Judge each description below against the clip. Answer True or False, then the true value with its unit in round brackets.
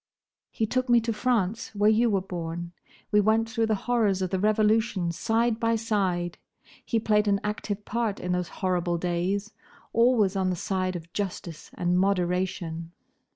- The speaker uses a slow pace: False (165 wpm)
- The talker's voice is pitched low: False (200 Hz)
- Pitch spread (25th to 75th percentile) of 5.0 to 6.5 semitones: False (3.6 semitones)